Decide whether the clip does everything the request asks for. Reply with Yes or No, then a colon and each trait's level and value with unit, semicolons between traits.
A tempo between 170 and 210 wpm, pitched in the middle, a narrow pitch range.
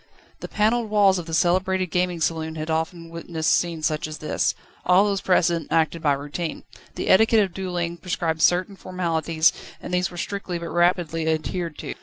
Yes: average, 180 wpm; medium, 170 Hz; narrow, 2.3 semitones